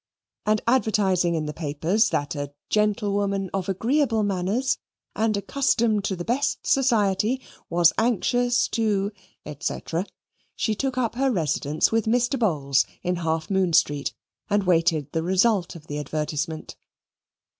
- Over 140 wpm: No, slow, 135 wpm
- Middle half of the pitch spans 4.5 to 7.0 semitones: Yes, wide, 5.6 semitones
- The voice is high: Yes, high, 195 Hz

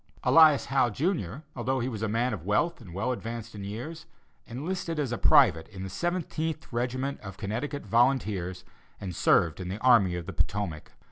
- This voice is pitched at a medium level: No, low, 120 Hz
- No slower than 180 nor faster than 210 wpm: Yes, average, 185 wpm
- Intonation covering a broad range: Yes, wide, 5.9 semitones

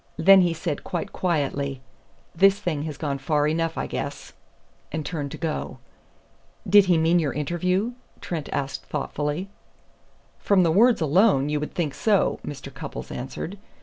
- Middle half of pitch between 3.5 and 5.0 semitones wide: Yes, average, 3.9 semitones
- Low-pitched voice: No, medium, 160 Hz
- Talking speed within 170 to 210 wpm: No, average, 155 wpm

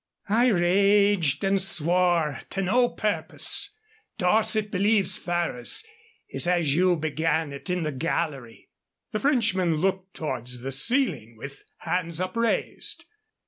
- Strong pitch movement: No, average, 4.6 semitones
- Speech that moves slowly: Yes, slow, 120 wpm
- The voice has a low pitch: No, medium, 180 Hz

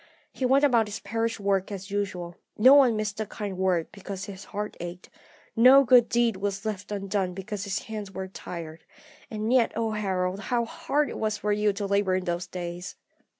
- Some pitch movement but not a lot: Yes, average, 3.0 semitones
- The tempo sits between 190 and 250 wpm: Yes, average, 195 wpm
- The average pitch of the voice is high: Yes, high, 205 Hz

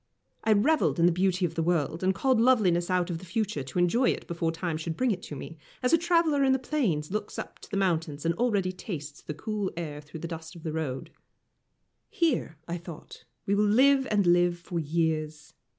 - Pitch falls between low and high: Yes, medium, 175 Hz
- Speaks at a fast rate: Yes, fast, 220 wpm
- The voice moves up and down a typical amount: Yes, average, 4.9 semitones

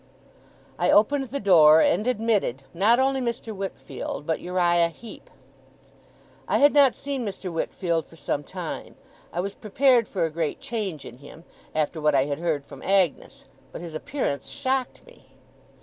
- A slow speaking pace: No, average, 165 wpm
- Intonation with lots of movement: Yes, wide, 6.8 semitones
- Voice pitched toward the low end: No, high, 190 Hz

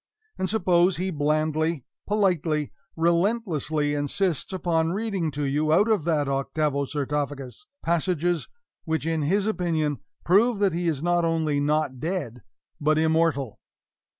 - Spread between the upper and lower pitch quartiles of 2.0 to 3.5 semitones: Yes, average, 3.2 semitones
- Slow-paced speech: Yes, slow, 130 wpm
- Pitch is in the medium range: Yes, medium, 160 Hz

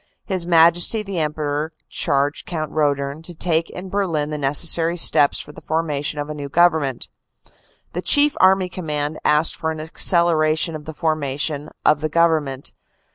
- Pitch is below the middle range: No, medium, 155 Hz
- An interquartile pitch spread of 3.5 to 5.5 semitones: No, narrow, 2.4 semitones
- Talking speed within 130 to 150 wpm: No, average, 160 wpm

